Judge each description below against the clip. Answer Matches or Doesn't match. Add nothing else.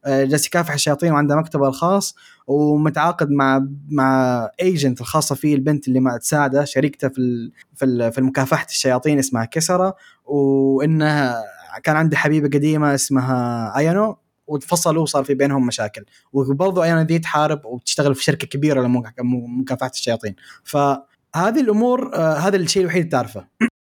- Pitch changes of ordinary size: Matches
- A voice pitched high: Doesn't match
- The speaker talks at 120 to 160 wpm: Matches